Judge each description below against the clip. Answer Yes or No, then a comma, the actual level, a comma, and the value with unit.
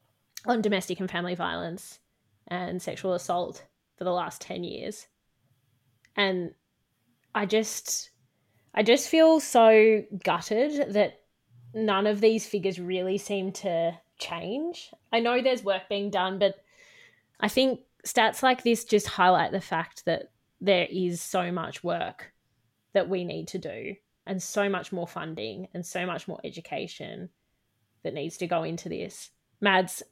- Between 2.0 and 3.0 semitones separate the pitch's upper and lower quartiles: No, average, 3.8 semitones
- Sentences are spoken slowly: No, average, 145 wpm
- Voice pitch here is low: No, high, 190 Hz